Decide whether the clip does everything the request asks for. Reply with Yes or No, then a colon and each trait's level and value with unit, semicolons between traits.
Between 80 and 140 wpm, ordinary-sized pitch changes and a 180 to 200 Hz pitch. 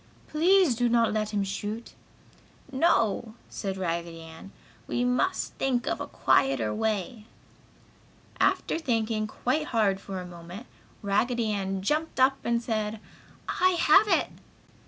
No: slow, 135 wpm; average, 4.4 semitones; high, 220 Hz